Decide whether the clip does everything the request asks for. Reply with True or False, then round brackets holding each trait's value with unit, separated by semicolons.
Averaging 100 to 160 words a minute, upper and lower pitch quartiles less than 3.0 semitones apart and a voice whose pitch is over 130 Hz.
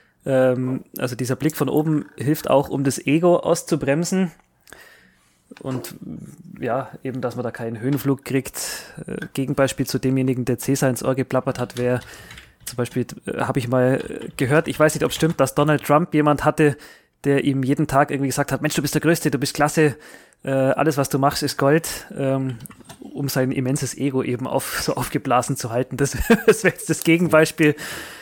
False (180 wpm; 2.6 semitones; 140 Hz)